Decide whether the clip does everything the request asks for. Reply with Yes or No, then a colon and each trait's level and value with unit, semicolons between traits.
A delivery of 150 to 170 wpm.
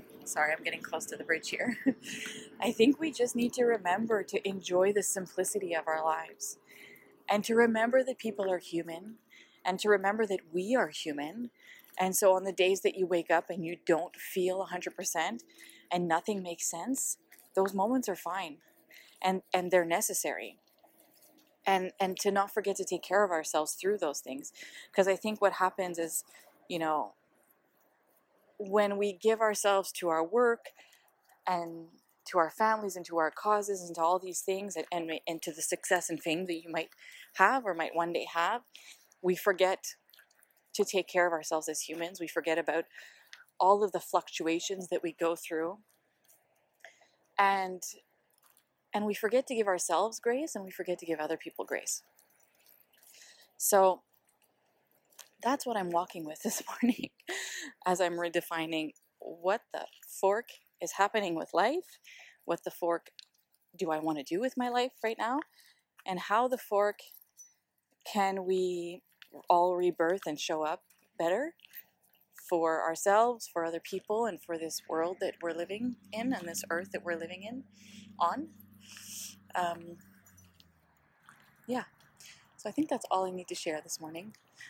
Yes: average, 165 wpm